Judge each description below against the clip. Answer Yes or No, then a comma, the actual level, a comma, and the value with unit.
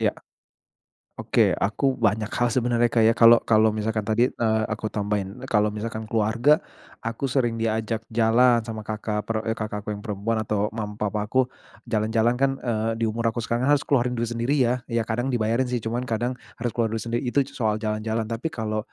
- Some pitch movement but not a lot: No, narrow, 1.8 semitones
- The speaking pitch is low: Yes, low, 115 Hz